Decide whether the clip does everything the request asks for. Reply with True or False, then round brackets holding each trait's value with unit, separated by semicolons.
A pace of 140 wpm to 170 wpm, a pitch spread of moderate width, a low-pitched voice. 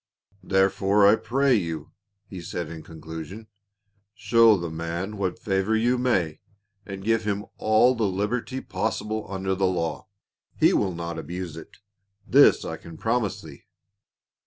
True (150 wpm; 4.4 semitones; 95 Hz)